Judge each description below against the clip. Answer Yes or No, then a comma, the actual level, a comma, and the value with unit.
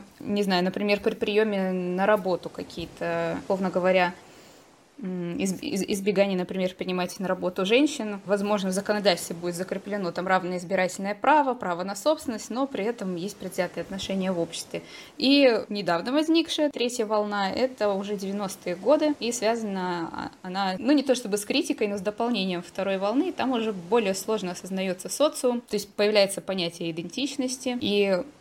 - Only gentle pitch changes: No, average, 4.2 semitones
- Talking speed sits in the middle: Yes, average, 150 wpm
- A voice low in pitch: No, high, 200 Hz